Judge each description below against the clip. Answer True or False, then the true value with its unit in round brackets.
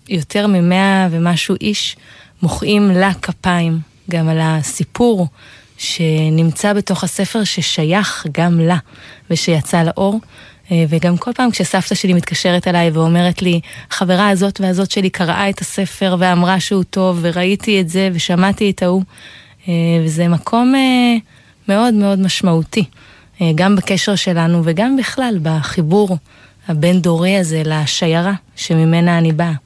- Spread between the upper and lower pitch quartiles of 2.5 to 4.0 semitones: True (3.0 semitones)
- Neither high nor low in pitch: True (180 Hz)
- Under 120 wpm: False (125 wpm)